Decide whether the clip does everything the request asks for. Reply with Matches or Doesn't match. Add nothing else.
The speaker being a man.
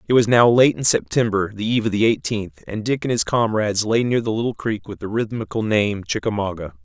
Matches